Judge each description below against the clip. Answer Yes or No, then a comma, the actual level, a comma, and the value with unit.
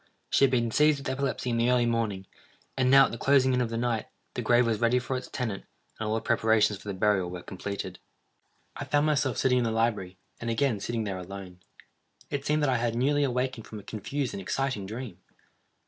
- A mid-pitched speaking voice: No, low, 115 Hz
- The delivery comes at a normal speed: No, fast, 225 wpm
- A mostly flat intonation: No, average, 3.8 semitones